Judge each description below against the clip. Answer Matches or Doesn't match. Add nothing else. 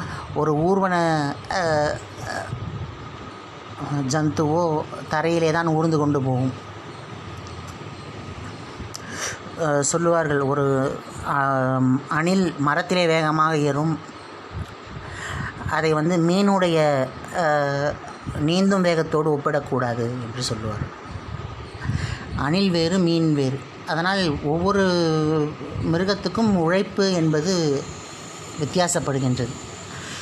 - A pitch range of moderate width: Matches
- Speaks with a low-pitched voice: Doesn't match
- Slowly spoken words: Matches